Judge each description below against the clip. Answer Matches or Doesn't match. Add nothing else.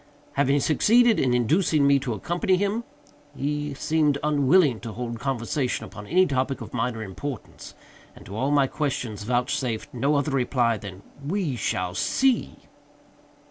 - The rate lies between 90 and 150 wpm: Matches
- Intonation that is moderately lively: Matches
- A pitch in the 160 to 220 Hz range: Doesn't match